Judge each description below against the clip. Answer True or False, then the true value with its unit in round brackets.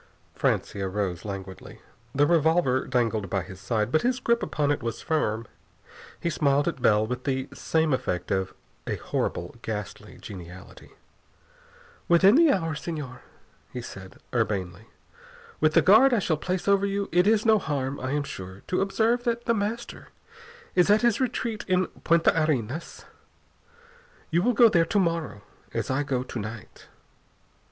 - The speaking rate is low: False (160 wpm)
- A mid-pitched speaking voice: True (145 Hz)